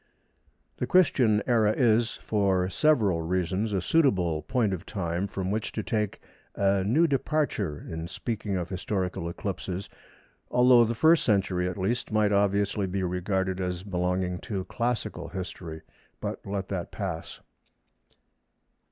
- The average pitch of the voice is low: Yes, low, 100 Hz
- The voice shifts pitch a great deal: No, average, 3.3 semitones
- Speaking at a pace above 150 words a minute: No, slow, 135 wpm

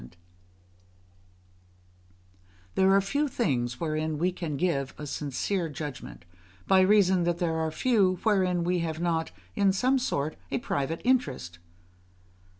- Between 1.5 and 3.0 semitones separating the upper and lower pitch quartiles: No, average, 4.1 semitones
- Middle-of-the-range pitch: Yes, medium, 175 Hz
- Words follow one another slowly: Yes, slow, 130 wpm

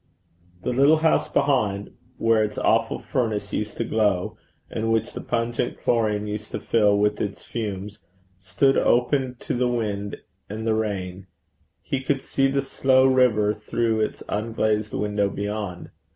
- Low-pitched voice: Yes, low, 110 Hz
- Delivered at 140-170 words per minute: Yes, average, 150 wpm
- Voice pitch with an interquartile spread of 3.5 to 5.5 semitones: No, average, 3.0 semitones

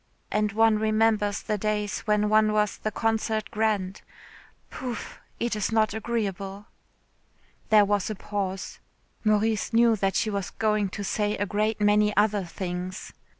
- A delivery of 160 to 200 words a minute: No, average, 150 wpm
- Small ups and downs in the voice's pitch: Yes, narrow, 1.2 semitones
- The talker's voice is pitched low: No, high, 210 Hz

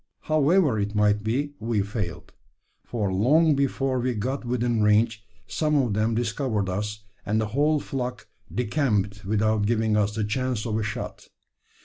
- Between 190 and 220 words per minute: No, average, 155 wpm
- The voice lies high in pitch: No, low, 110 Hz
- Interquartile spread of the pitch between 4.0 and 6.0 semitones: No, average, 3.6 semitones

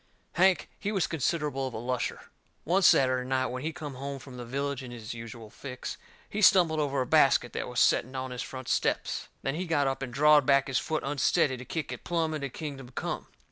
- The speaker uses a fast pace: Yes, fast, 220 wpm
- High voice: No, low, 135 Hz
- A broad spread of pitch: No, average, 3.4 semitones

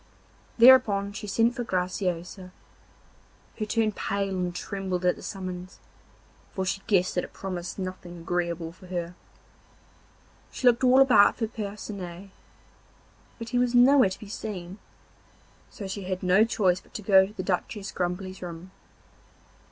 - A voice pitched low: No, high, 190 Hz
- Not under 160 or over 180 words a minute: No, average, 150 wpm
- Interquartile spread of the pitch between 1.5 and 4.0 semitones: Yes, average, 2.9 semitones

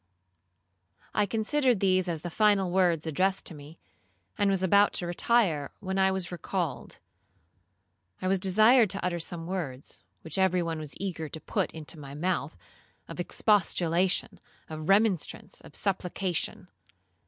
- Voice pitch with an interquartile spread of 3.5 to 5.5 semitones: No, average, 3.1 semitones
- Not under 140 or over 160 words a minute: Yes, average, 145 wpm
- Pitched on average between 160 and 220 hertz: Yes, medium, 185 Hz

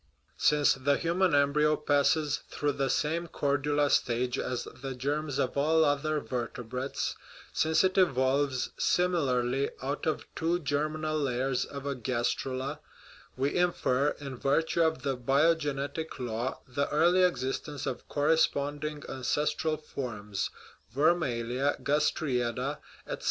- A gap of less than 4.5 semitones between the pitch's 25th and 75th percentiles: Yes, average, 2.9 semitones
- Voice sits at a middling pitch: Yes, medium, 145 Hz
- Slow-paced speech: Yes, slow, 125 wpm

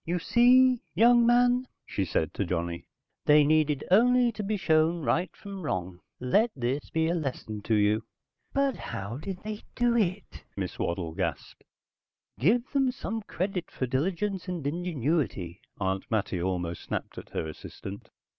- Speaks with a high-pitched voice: No, medium, 160 Hz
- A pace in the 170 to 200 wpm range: No, average, 155 wpm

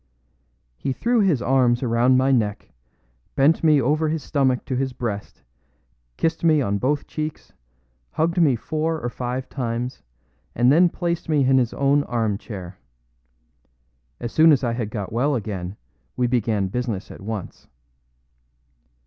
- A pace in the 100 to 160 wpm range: Yes, average, 150 wpm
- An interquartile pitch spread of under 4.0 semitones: No, average, 4.5 semitones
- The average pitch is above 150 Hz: No, low, 130 Hz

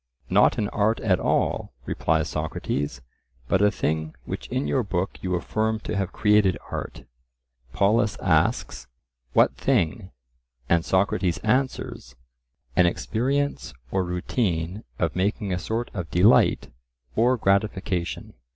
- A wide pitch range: No, average, 4.0 semitones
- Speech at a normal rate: No, slow, 125 wpm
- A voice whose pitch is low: Yes, low, 100 Hz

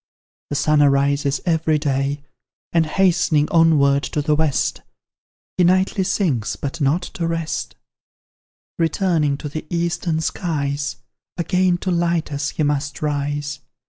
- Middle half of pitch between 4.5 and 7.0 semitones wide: No, average, 3.0 semitones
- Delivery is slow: Yes, slow, 130 wpm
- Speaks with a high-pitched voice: No, medium, 150 Hz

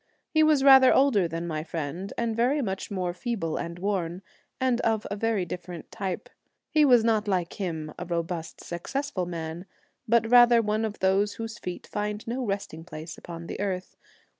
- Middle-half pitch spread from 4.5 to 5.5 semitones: Yes, average, 5.1 semitones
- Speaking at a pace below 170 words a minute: No, average, 180 wpm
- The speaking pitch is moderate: No, high, 200 Hz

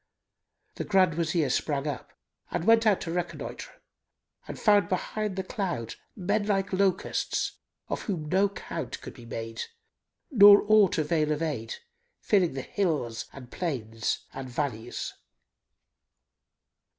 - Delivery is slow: Yes, slow, 130 wpm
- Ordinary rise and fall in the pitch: No, wide, 6.3 semitones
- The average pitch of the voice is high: No, medium, 170 Hz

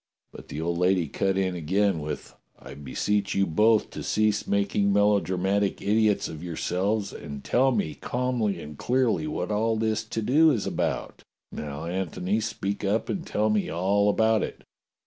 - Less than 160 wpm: No, average, 165 wpm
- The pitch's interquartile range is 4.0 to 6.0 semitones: No, average, 3.5 semitones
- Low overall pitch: Yes, low, 100 Hz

